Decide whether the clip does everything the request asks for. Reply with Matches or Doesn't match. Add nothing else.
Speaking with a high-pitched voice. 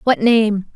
Matches